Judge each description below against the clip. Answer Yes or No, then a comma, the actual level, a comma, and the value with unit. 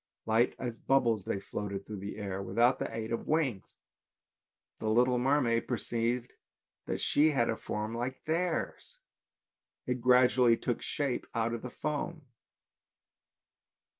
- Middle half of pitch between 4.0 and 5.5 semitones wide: No, average, 2.7 semitones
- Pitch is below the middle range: Yes, low, 120 Hz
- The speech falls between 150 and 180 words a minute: No, slow, 135 wpm